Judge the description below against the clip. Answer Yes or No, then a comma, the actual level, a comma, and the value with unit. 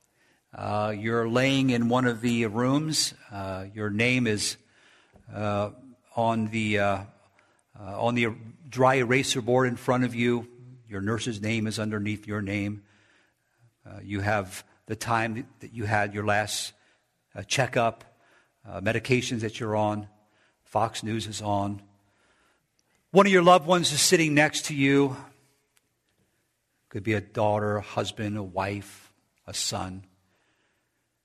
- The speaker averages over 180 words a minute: No, average, 140 wpm